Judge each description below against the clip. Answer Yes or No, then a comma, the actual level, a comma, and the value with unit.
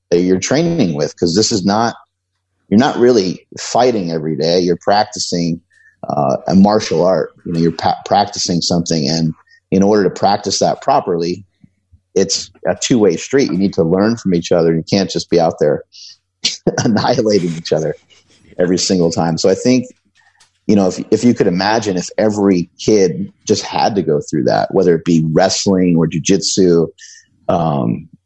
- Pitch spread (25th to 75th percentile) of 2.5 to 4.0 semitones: Yes, average, 3.2 semitones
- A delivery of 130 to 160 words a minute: No, average, 175 wpm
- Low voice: Yes, very low, 90 Hz